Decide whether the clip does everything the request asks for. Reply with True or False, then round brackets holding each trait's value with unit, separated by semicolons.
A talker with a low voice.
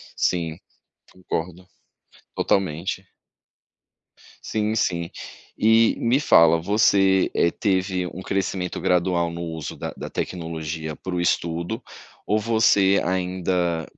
True (90 Hz)